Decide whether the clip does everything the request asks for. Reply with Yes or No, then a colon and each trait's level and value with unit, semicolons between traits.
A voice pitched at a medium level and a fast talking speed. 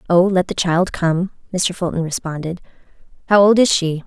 No: medium, 180 Hz; average, 175 wpm